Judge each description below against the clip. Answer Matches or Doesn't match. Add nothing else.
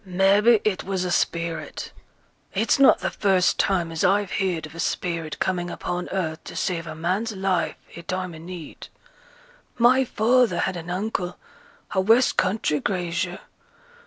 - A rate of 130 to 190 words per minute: Matches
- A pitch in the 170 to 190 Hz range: Matches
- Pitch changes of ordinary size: Matches